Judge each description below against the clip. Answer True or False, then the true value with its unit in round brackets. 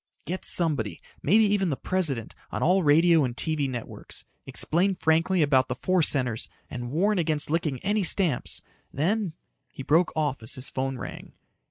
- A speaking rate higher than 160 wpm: True (170 wpm)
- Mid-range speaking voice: True (155 Hz)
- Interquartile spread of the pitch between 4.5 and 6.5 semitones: True (5.4 semitones)